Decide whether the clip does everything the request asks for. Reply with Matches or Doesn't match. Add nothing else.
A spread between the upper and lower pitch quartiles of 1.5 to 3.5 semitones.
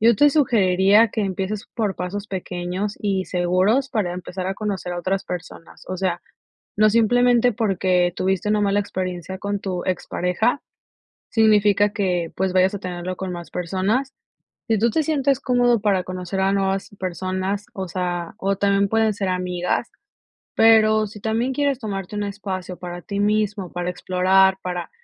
Matches